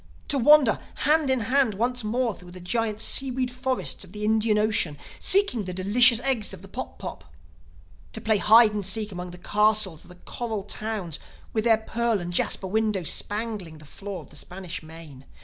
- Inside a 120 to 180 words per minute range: No, average, 190 wpm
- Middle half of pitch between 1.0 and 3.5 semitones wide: No, average, 4.2 semitones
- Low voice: No, high, 215 Hz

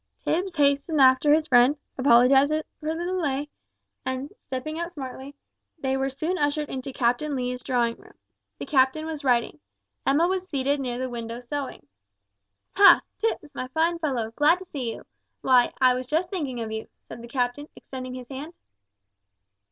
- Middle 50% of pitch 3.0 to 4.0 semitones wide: Yes, average, 3.5 semitones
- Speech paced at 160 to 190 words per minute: Yes, average, 165 wpm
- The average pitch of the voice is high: Yes, very high, 275 Hz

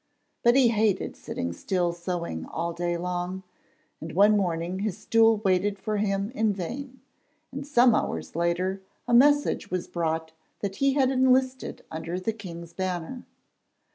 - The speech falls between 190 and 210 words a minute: No, average, 150 wpm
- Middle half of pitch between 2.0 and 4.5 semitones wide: No, average, 5.3 semitones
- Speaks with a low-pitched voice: No, high, 190 Hz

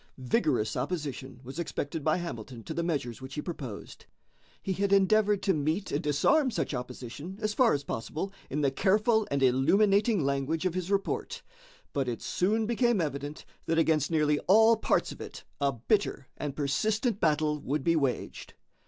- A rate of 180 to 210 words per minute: No, average, 170 wpm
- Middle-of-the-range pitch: Yes, medium, 155 Hz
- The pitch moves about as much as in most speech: No, wide, 6.2 semitones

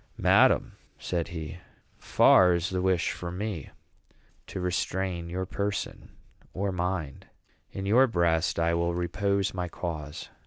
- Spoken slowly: Yes, slow, 130 wpm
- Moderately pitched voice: No, very low, 90 Hz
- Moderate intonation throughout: No, narrow, 2.0 semitones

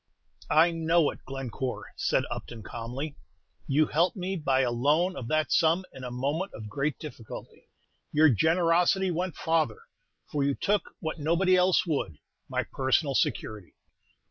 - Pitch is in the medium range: Yes, medium, 155 Hz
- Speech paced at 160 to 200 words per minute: No, average, 150 wpm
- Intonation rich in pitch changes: No, average, 4.5 semitones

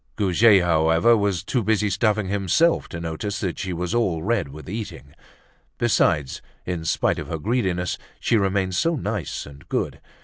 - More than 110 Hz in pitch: No, very low, 95 Hz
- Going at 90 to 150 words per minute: No, average, 165 wpm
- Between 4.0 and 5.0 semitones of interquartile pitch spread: Yes, average, 4.5 semitones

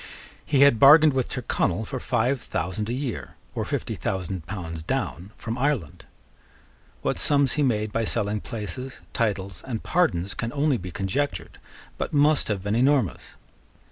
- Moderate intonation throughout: No, wide, 5.9 semitones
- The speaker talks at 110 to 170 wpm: Yes, average, 155 wpm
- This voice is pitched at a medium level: No, low, 115 Hz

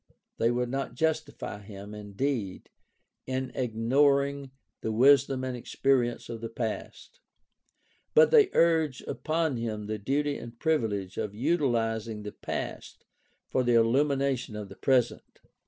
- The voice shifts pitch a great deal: No, average, 3.9 semitones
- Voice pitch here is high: No, low, 125 Hz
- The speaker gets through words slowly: Yes, slow, 130 wpm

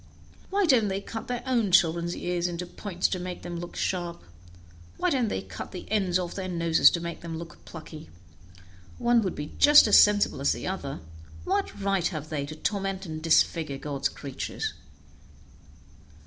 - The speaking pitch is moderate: Yes, medium, 180 Hz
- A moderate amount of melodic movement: Yes, average, 3.7 semitones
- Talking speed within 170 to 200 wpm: Yes, average, 175 wpm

